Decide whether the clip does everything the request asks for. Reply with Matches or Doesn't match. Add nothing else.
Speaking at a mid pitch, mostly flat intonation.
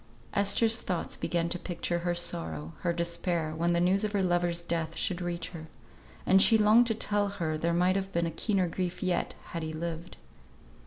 Matches